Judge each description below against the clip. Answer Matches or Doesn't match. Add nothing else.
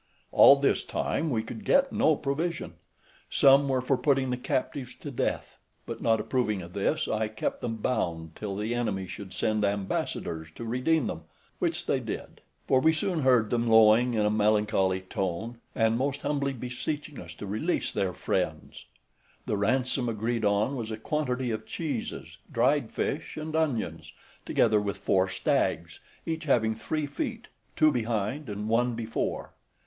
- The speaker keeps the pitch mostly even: Doesn't match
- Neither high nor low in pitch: Doesn't match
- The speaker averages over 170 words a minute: Doesn't match